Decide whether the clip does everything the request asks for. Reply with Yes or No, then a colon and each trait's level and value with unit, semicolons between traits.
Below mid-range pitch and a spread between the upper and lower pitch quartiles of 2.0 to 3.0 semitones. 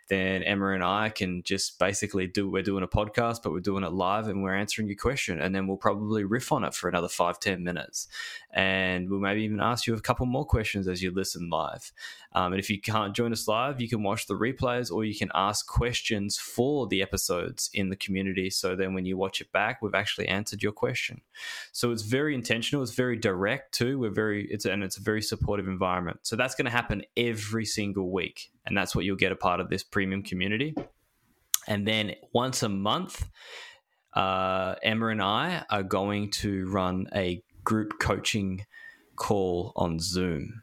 Yes: low, 100 Hz; average, 2.7 semitones